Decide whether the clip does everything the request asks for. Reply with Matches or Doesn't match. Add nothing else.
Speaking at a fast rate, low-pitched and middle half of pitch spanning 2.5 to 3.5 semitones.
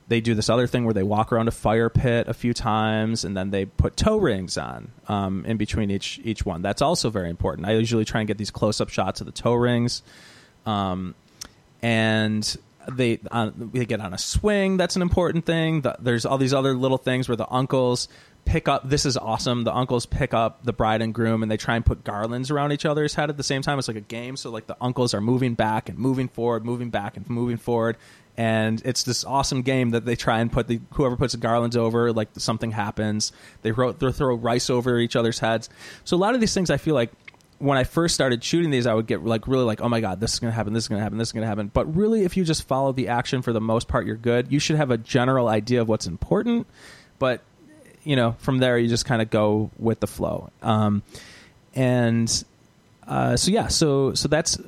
Matches